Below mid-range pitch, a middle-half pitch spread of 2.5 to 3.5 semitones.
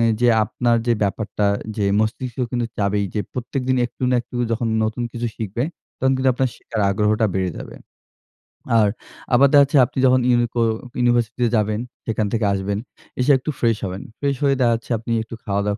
Yes: low, 115 Hz; average, 2.8 semitones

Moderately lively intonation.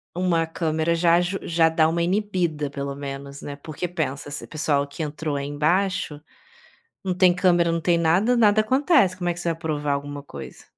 Yes: average, 3.5 semitones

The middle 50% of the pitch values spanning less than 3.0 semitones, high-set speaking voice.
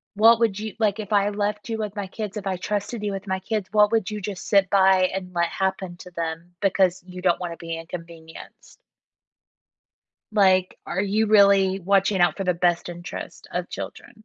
Yes: narrow, 2.4 semitones; high, 195 Hz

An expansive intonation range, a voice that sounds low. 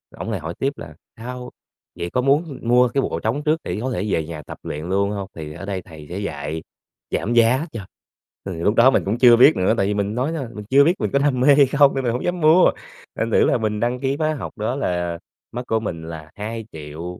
Yes: wide, 6.8 semitones; low, 115 Hz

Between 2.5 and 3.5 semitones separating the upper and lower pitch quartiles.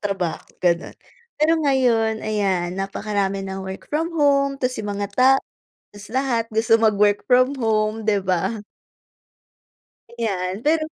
No: average, 4.5 semitones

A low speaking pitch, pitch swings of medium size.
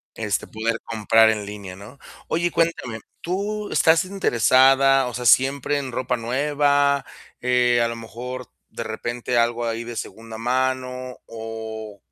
Yes: low, 125 Hz; average, 3.2 semitones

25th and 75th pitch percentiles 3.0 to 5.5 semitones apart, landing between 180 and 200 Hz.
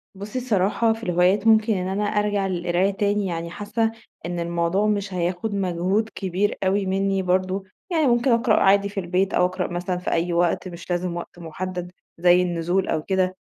No: narrow, 2.6 semitones; high, 190 Hz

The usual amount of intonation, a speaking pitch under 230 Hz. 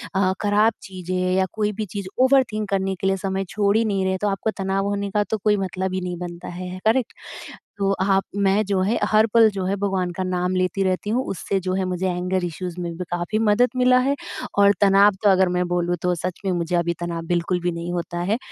No: narrow, 2.3 semitones; high, 190 Hz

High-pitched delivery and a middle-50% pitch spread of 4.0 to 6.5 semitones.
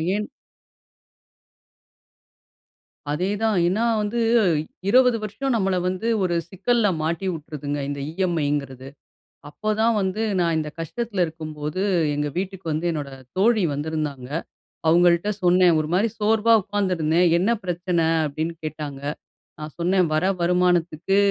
No: medium, 175 Hz; average, 4.6 semitones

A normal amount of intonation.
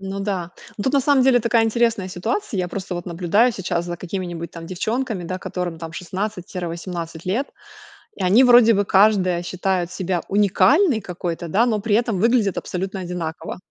Yes: average, 4.1 semitones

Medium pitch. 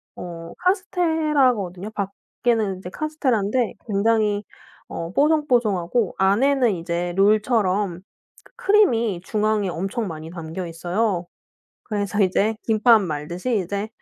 No: high, 210 Hz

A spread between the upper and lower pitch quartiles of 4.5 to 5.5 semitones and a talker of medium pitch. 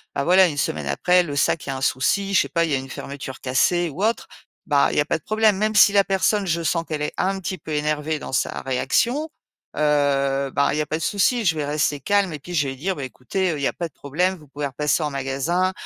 Yes: average, 5.0 semitones; medium, 155 Hz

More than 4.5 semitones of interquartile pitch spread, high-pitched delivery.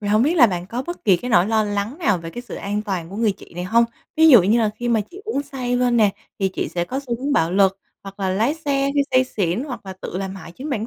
Yes: average, 4.9 semitones; high, 220 Hz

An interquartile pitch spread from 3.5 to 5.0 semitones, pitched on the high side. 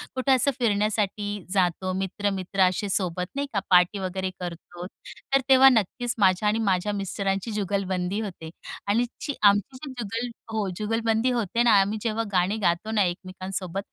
No: average, 3.1 semitones; high, 200 Hz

